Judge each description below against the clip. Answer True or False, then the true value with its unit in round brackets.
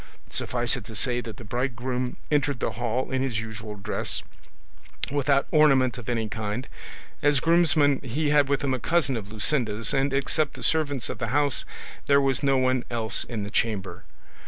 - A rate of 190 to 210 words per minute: False (180 wpm)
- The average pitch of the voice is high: False (130 Hz)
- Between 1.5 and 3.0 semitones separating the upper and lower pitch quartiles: False (3.7 semitones)